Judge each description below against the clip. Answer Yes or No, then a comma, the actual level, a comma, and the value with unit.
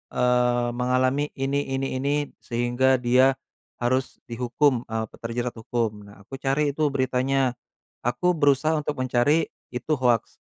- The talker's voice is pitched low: Yes, low, 130 Hz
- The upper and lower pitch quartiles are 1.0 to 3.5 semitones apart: Yes, narrow, 2.4 semitones